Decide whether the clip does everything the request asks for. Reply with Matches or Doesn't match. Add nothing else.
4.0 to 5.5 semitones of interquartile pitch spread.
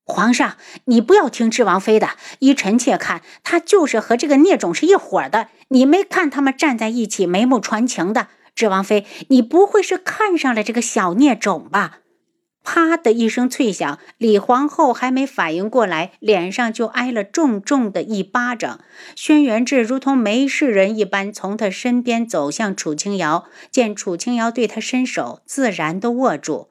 Matches